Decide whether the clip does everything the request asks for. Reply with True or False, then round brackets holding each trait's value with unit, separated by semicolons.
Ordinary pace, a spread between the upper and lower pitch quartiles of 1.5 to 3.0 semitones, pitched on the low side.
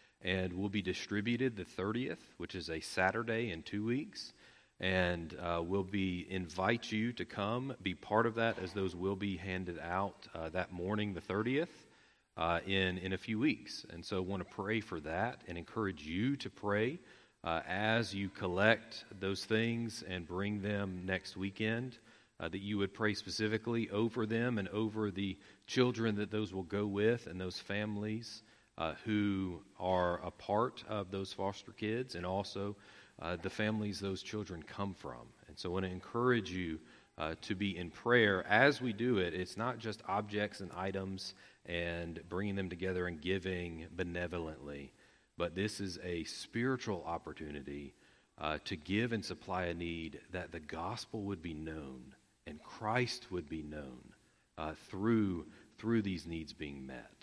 False (170 wpm; 3.4 semitones; 95 Hz)